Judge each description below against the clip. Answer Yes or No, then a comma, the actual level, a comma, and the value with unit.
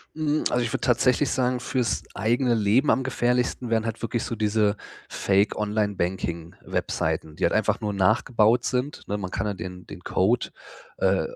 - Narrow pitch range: No, average, 3.3 semitones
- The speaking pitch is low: Yes, low, 110 Hz